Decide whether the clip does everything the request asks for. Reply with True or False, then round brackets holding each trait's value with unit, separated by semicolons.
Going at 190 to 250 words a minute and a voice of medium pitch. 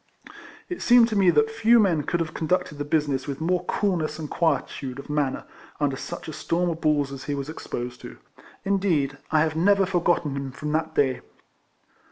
True (195 wpm; 155 Hz)